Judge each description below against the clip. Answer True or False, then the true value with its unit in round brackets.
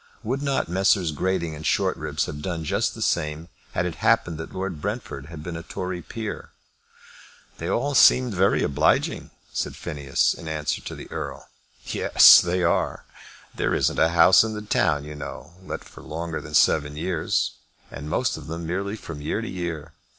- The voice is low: True (85 Hz)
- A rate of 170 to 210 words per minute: True (185 wpm)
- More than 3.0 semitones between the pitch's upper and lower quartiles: True (3.6 semitones)